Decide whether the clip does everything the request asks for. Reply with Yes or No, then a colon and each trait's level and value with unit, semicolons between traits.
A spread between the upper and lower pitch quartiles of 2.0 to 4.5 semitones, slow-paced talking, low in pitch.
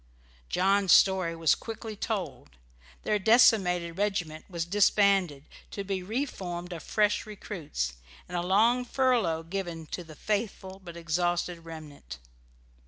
No: average, 3.7 semitones; slow, 125 wpm; medium, 180 Hz